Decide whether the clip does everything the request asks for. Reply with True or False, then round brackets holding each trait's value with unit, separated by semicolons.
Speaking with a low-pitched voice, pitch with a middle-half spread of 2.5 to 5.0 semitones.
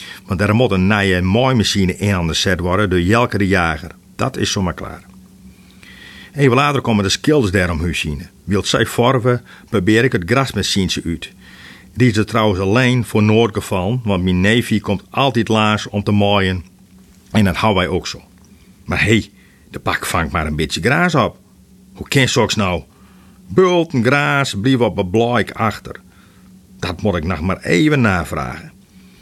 True (100 Hz; 3.6 semitones)